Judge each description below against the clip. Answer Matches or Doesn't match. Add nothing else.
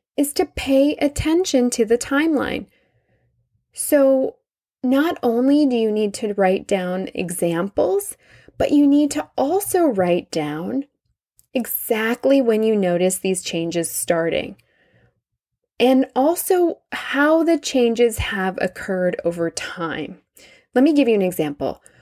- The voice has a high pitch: Matches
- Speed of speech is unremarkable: Doesn't match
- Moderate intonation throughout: Doesn't match